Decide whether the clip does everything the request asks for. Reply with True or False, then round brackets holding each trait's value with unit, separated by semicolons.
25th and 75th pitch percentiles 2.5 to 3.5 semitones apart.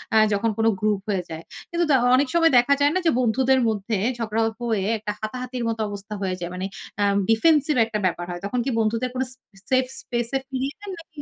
False (4.0 semitones)